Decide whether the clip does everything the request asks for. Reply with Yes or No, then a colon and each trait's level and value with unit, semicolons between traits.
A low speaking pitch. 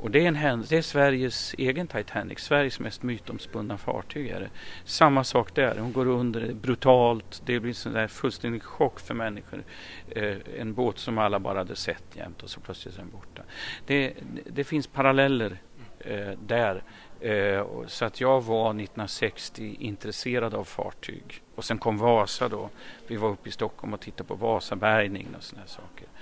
Yes: low, 115 Hz